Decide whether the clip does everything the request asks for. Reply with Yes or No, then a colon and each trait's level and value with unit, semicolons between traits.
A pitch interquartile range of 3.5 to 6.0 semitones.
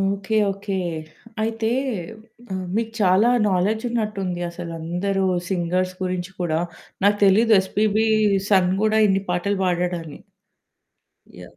No: average, 2.9 semitones